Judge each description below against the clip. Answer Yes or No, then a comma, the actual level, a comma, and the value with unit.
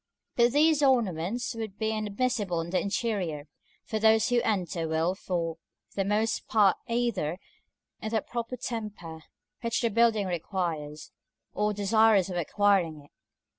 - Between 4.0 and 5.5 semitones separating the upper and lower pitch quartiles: Yes, average, 4.6 semitones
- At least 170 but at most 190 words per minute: No, average, 145 wpm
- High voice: Yes, high, 205 Hz